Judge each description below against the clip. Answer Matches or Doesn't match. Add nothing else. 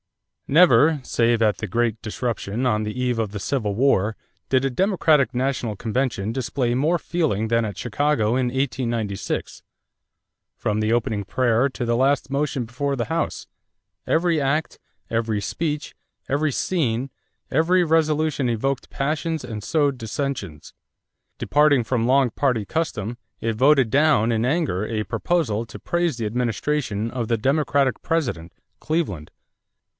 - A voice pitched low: Matches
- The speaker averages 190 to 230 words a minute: Doesn't match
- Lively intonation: Doesn't match